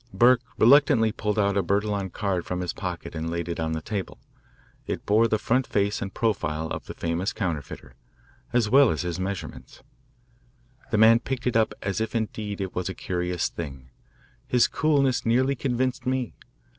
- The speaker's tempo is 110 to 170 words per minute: No, average, 180 wpm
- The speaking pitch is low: Yes, low, 105 Hz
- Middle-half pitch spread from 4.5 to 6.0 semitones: Yes, average, 5.0 semitones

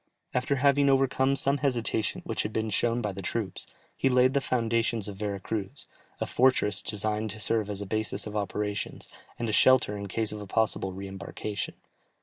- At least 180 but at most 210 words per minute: Yes, average, 190 wpm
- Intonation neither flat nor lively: Yes, average, 3.6 semitones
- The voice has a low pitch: Yes, low, 110 Hz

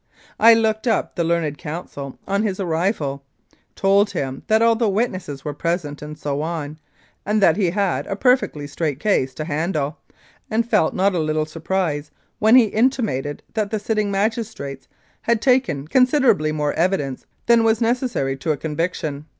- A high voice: No, medium, 175 Hz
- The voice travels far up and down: Yes, wide, 6.5 semitones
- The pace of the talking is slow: No, average, 165 wpm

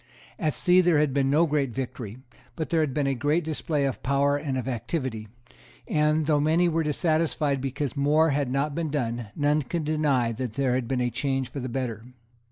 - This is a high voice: No, medium, 140 Hz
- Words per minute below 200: No, fast, 205 wpm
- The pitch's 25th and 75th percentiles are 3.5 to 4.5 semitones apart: No, average, 3.0 semitones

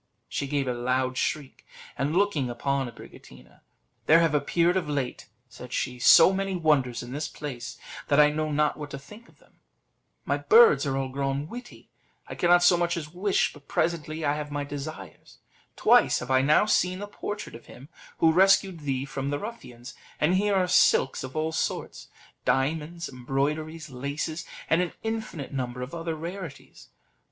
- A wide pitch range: No, average, 4.2 semitones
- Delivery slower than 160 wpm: No, average, 180 wpm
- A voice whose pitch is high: No, medium, 150 Hz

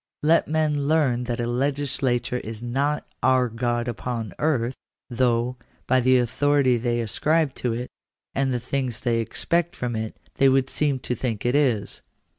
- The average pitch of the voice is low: Yes, low, 125 Hz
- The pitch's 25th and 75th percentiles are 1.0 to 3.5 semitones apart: Yes, average, 2.8 semitones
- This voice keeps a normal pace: Yes, average, 170 wpm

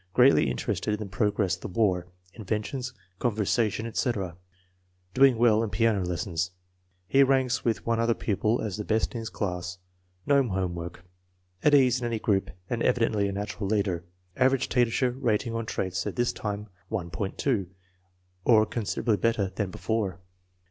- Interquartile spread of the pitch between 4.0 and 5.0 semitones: No, average, 3.6 semitones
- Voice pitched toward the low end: Yes, low, 110 Hz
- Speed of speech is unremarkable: Yes, average, 160 wpm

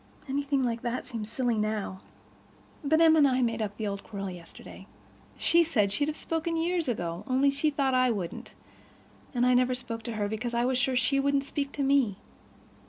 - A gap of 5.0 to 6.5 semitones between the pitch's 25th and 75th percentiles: No, average, 4.3 semitones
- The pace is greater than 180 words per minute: Yes, average, 200 wpm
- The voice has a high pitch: Yes, very high, 250 Hz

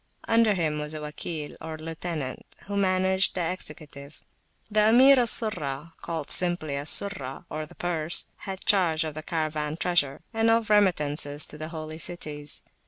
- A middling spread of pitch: Yes, average, 3.9 semitones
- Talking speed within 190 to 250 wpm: No, average, 155 wpm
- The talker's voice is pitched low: No, medium, 160 Hz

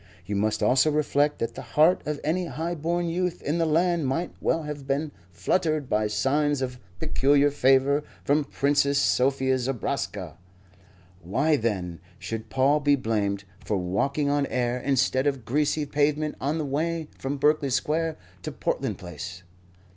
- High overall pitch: No, medium, 140 Hz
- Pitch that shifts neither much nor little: Yes, average, 3.3 semitones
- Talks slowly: No, average, 155 wpm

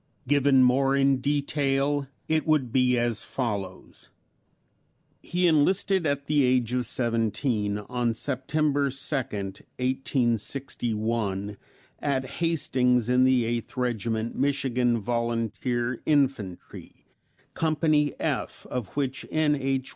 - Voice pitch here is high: No, low, 130 Hz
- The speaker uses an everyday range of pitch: Yes, average, 3.3 semitones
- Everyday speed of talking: No, slow, 105 wpm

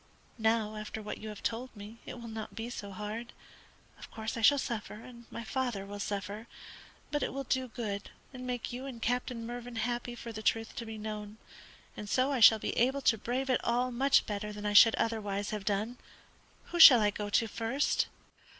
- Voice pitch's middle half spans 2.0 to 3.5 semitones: Yes, narrow, 2.6 semitones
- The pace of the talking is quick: Yes, fast, 210 wpm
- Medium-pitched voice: No, high, 225 Hz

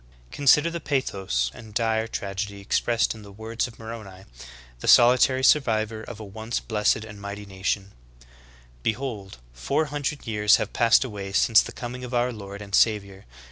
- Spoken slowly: No, average, 170 wpm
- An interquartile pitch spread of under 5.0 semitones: Yes, average, 3.3 semitones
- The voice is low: Yes, low, 110 Hz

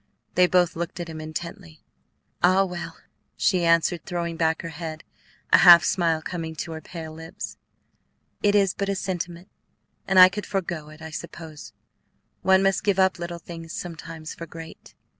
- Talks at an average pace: Yes, average, 170 wpm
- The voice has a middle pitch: Yes, medium, 170 Hz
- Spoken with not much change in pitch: Yes, narrow, 2.1 semitones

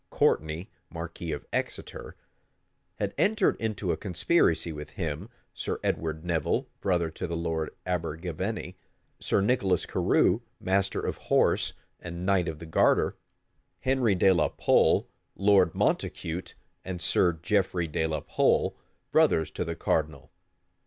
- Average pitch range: Yes, average, 3.2 semitones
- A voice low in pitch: Yes, very low, 85 Hz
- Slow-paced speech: Yes, slow, 130 wpm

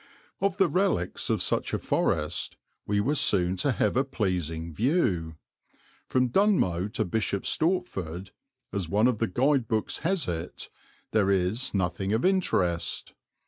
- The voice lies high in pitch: No, low, 105 Hz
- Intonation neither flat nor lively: No, wide, 7.5 semitones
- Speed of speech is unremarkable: Yes, average, 145 wpm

